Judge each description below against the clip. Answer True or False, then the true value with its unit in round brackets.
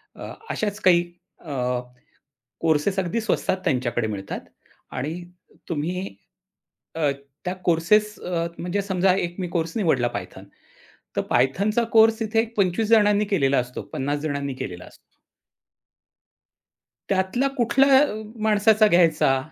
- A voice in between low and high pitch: True (180 Hz)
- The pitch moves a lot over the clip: True (6.0 semitones)